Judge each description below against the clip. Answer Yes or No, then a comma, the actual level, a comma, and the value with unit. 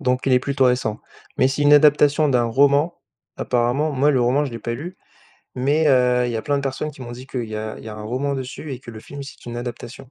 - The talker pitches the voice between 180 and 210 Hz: No, low, 130 Hz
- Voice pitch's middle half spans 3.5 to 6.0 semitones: No, average, 2.9 semitones